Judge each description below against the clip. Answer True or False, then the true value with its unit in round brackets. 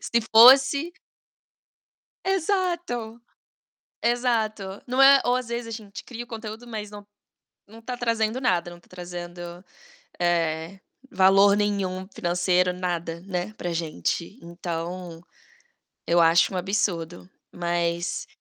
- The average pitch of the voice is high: True (195 Hz)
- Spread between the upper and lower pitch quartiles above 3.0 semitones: True (5.2 semitones)